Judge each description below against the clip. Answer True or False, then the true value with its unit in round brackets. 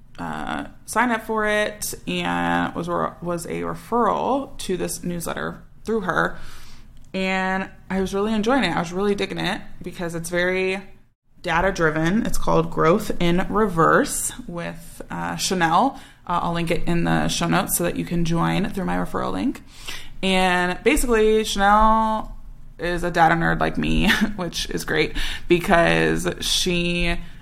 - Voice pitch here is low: False (170 Hz)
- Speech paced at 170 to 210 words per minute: False (155 wpm)